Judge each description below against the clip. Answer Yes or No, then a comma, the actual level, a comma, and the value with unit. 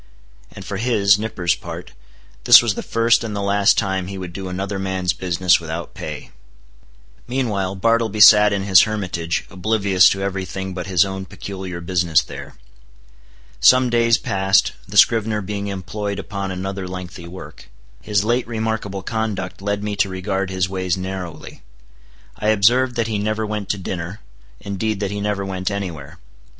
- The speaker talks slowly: No, average, 165 wpm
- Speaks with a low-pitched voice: Yes, low, 100 Hz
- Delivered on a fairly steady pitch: Yes, narrow, 2.2 semitones